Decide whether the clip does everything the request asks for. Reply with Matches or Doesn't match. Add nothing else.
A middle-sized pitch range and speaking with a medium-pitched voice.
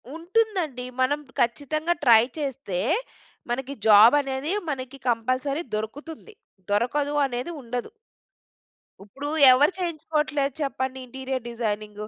Doesn't match